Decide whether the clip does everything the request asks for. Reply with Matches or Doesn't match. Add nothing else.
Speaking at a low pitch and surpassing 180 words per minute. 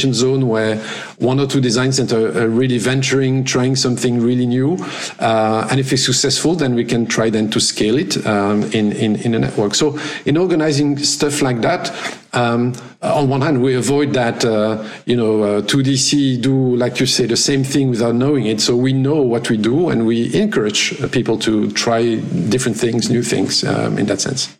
Matches